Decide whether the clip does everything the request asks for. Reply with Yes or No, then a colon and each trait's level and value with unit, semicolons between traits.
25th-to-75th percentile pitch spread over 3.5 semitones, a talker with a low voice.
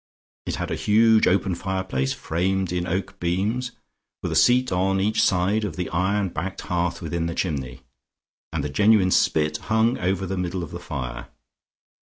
No: average, 2.8 semitones; very low, 95 Hz